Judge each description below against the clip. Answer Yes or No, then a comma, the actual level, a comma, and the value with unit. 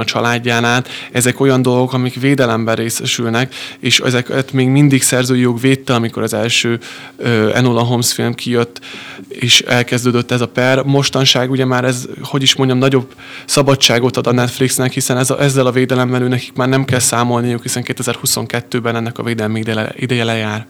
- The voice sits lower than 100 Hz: No, low, 125 Hz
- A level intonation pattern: Yes, narrow, 1.7 semitones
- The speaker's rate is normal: No, fast, 170 wpm